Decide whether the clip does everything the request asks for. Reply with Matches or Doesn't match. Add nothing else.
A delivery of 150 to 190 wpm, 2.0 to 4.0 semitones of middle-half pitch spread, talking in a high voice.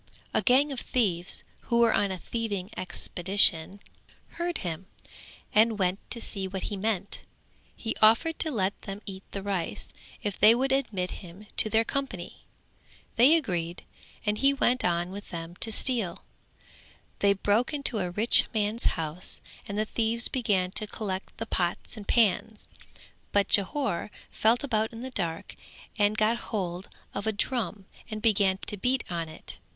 Matches